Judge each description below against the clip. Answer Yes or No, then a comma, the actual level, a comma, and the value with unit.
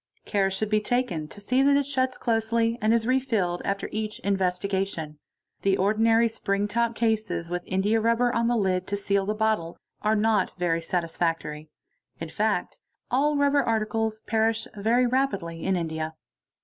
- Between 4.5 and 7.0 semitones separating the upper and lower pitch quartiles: No, average, 3.7 semitones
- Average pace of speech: Yes, average, 165 wpm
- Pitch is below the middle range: No, high, 215 Hz